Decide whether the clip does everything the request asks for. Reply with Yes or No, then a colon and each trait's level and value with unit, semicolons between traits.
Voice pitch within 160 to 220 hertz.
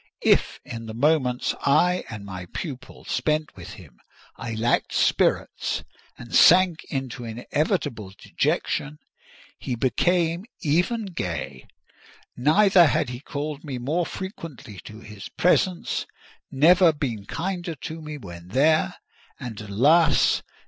No: medium, 140 Hz